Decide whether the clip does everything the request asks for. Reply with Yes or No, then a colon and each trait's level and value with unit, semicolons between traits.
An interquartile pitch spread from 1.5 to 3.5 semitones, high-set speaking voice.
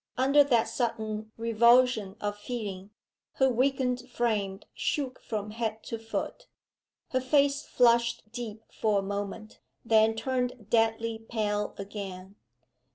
Yes: average, 2.9 semitones; high, 225 Hz